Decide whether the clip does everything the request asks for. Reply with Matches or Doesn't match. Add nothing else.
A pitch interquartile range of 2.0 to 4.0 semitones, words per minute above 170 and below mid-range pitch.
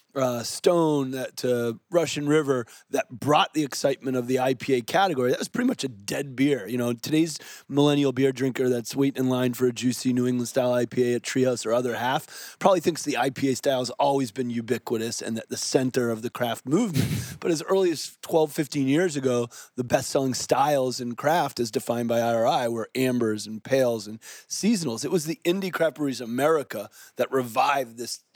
Matches